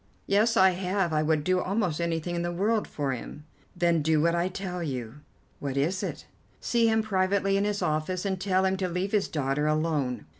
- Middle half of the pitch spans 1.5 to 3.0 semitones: No, average, 4.0 semitones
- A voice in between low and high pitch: Yes, medium, 180 Hz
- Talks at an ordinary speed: No, fast, 210 wpm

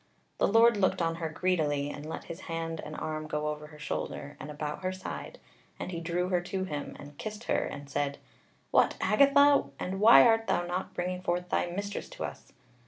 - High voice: No, medium, 175 Hz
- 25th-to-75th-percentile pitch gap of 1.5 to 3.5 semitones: No, average, 3.9 semitones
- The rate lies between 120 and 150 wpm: No, fast, 205 wpm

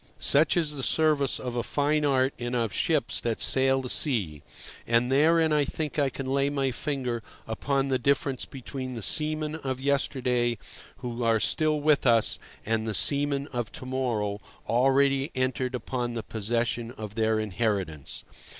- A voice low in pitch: Yes, low, 130 Hz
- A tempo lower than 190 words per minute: Yes, average, 165 wpm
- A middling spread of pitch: Yes, average, 3.2 semitones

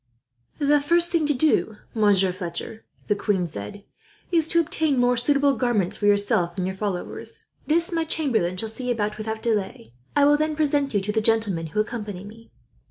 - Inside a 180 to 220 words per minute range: Yes, average, 185 wpm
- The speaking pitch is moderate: No, high, 220 Hz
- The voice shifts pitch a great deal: Yes, wide, 6.2 semitones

